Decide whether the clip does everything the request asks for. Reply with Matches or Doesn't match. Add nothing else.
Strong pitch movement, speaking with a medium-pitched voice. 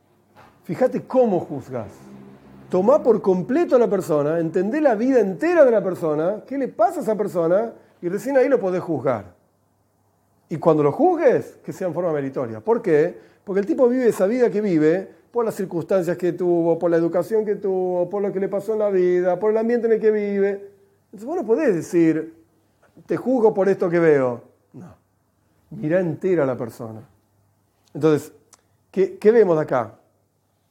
Matches